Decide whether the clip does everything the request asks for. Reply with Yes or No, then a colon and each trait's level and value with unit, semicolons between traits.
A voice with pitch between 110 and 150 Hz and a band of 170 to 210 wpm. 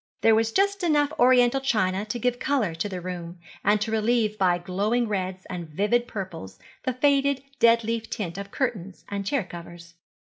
No: high, 215 Hz; average, 180 wpm